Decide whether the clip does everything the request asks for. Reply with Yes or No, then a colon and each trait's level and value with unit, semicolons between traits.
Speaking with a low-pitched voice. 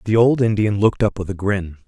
Yes: low, 105 Hz